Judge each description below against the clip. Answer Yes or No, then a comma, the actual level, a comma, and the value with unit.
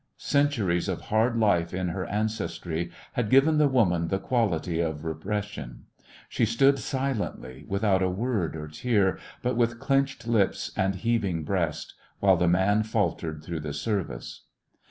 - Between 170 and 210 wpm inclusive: No, average, 155 wpm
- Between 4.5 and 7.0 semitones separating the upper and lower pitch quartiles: Yes, wide, 5.6 semitones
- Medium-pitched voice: No, low, 100 Hz